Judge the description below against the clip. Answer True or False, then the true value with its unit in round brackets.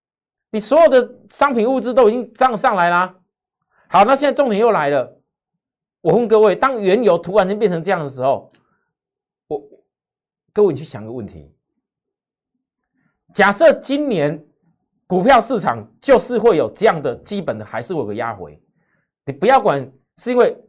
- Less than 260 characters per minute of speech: True (240 characters per minute)